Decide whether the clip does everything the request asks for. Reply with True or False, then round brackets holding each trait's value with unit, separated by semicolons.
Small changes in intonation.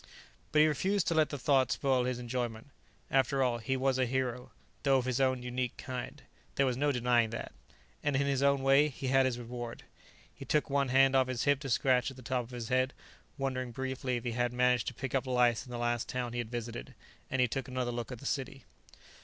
True (1.7 semitones)